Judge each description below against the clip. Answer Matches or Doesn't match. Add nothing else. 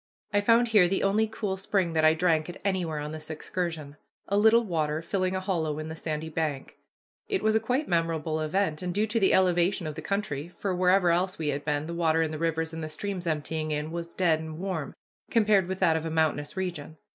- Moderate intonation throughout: Matches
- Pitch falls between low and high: Matches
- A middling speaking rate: Doesn't match